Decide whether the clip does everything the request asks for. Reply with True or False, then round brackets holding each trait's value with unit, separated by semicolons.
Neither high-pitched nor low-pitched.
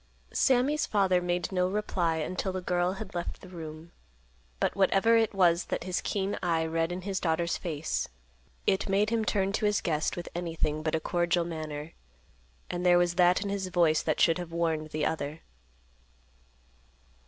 True (175 Hz)